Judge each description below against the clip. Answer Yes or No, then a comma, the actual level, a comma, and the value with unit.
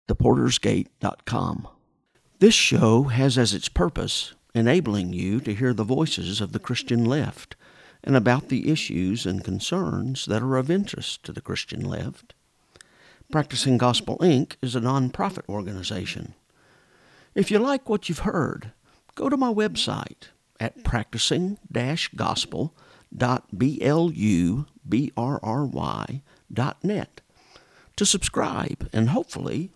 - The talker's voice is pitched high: No, low, 125 Hz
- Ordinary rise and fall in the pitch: No, wide, 5.9 semitones